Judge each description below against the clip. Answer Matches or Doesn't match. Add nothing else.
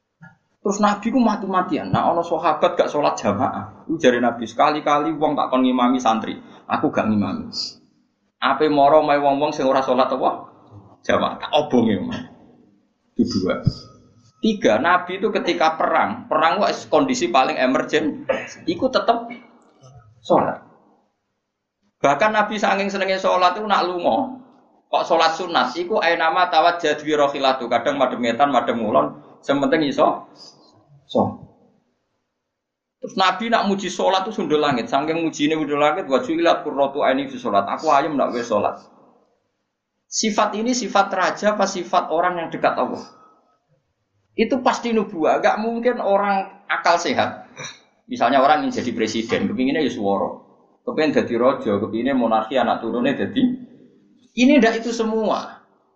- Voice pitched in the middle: Matches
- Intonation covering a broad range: Matches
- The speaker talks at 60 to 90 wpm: Doesn't match